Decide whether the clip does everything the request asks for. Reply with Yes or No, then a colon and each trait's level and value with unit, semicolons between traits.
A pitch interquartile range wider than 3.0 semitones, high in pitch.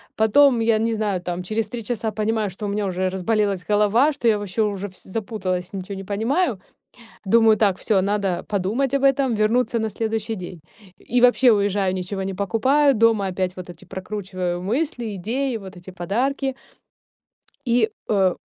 Yes: average, 3.4 semitones; high, 210 Hz